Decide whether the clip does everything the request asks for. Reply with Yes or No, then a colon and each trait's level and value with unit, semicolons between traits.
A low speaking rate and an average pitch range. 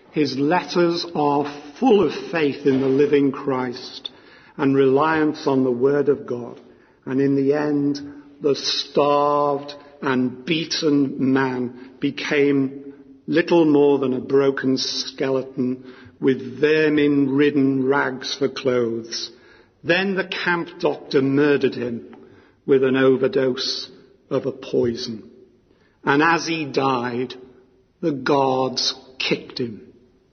No: slow, 115 wpm; narrow, 1.8 semitones